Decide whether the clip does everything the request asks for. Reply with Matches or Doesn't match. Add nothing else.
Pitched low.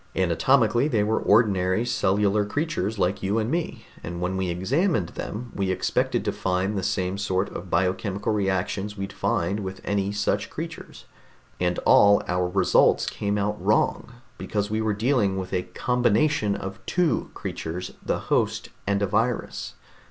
Matches